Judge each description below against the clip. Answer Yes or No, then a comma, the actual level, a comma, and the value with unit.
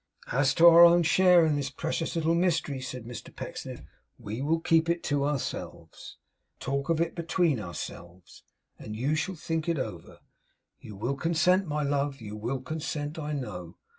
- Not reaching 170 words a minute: No, average, 175 wpm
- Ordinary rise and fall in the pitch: Yes, average, 4.6 semitones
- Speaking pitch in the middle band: Yes, medium, 145 Hz